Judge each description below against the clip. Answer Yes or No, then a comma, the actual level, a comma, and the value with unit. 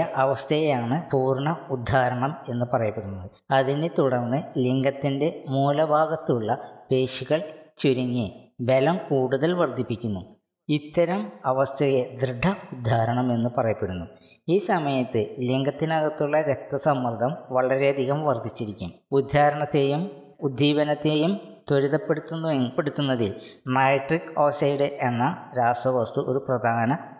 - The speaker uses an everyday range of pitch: Yes, average, 3.3 semitones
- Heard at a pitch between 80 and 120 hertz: No, low, 135 Hz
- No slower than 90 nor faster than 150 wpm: No, average, 75 wpm